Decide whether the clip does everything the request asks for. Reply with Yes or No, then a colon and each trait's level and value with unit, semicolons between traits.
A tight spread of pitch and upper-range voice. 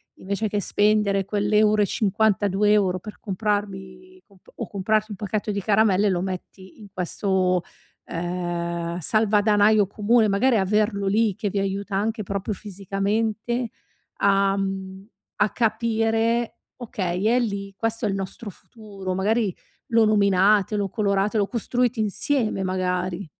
Yes: narrow, 2.1 semitones; high, 205 Hz